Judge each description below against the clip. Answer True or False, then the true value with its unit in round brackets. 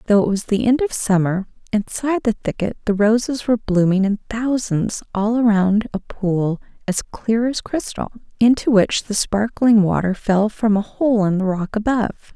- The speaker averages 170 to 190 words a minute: True (180 wpm)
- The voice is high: True (215 Hz)